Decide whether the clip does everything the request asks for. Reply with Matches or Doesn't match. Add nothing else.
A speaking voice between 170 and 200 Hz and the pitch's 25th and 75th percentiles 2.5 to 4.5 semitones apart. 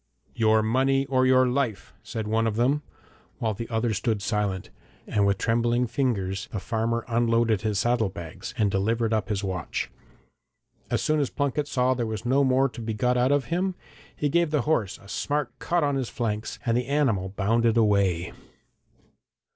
Doesn't match